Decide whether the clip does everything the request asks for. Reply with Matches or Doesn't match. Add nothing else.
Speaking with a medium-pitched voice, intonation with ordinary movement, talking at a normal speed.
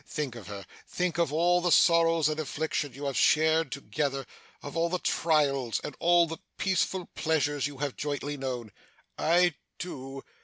Matches